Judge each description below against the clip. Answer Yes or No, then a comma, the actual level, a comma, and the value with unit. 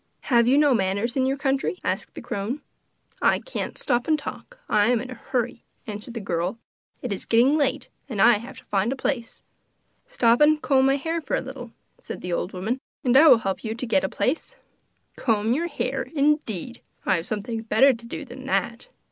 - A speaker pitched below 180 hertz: No, high, 245 Hz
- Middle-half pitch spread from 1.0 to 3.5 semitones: No, average, 3.9 semitones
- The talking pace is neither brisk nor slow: No, fast, 210 wpm